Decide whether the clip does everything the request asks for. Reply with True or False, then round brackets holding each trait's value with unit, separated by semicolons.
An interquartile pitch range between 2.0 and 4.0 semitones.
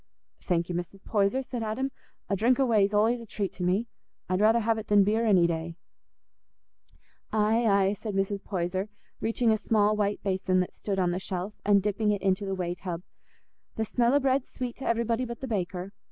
True (3.1 semitones)